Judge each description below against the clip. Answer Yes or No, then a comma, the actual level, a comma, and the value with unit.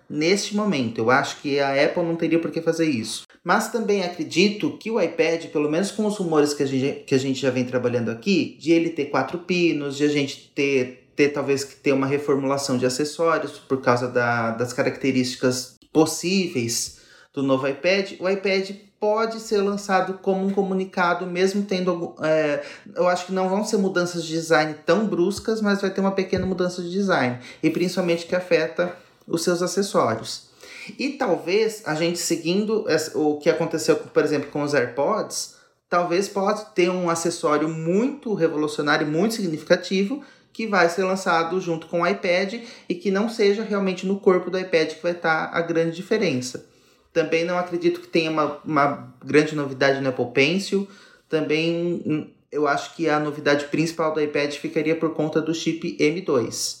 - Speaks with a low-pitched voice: No, medium, 165 Hz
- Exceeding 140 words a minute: Yes, average, 180 wpm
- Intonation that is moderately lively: Yes, average, 4.3 semitones